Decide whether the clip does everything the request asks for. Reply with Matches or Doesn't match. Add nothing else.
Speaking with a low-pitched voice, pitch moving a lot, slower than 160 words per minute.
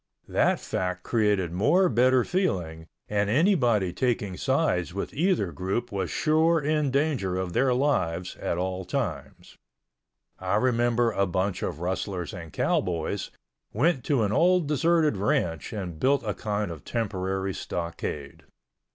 Matches